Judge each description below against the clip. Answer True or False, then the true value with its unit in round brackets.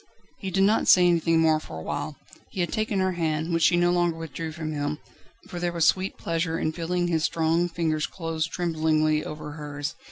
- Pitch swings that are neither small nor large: False (2.0 semitones)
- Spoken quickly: True (210 wpm)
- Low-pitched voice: False (165 Hz)